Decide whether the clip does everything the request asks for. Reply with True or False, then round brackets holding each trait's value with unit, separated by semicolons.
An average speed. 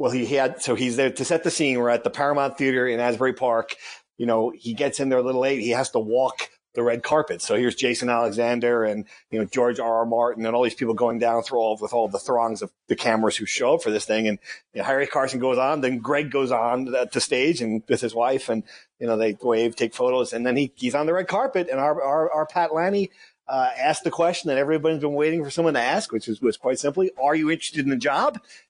False (270 wpm)